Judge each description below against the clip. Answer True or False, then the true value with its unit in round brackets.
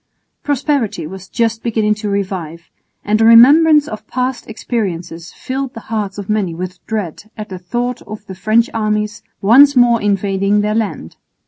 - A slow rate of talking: False (160 wpm)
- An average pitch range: True (3.2 semitones)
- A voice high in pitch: True (215 Hz)